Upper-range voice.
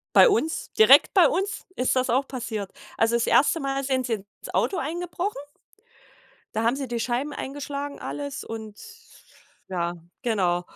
Yes: very high, 265 Hz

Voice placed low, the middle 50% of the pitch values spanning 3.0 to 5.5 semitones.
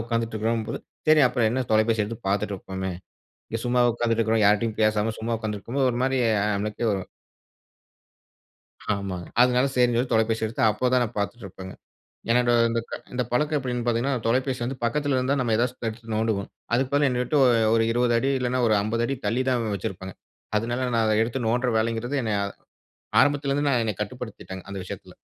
No: low, 115 Hz; narrow, 2.6 semitones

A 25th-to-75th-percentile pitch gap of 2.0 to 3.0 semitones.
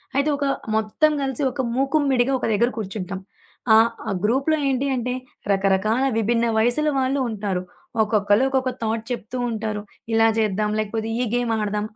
No: average, 3.6 semitones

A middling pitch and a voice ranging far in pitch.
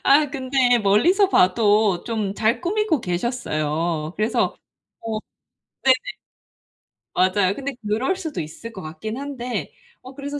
No: high, 230 Hz; wide, 6.4 semitones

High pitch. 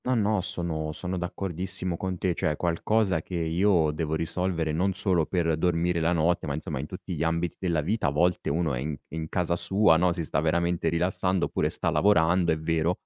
No: very low, 85 Hz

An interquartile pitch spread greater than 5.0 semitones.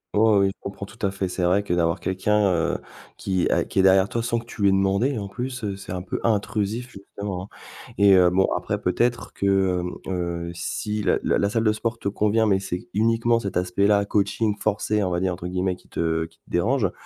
No: average, 2.8 semitones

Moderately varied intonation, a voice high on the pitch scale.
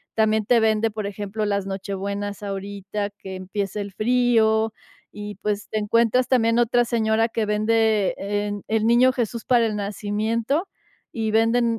No: narrow, 2.0 semitones; high, 215 Hz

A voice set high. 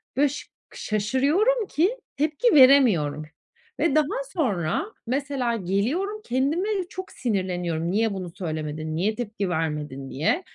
Yes: high, 235 Hz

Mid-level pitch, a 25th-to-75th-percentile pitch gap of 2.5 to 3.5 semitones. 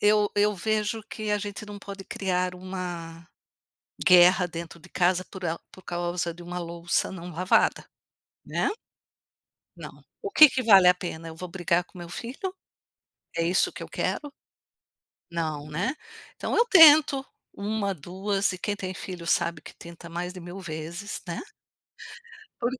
Yes: medium, 180 Hz; average, 3.2 semitones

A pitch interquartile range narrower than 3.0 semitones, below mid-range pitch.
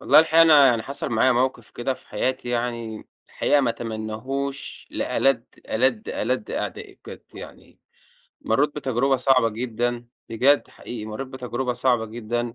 Yes: narrow, 2.5 semitones; low, 120 Hz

